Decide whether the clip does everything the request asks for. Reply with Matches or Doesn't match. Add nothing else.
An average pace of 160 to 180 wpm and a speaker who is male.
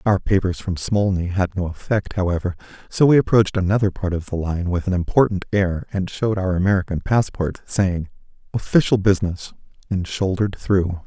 Matches